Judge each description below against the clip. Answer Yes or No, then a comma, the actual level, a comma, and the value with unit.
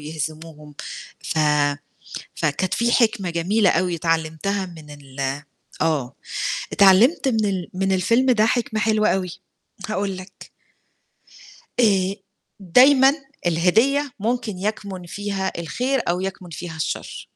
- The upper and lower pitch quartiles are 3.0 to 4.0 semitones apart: No, average, 4.7 semitones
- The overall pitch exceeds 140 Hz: Yes, high, 190 Hz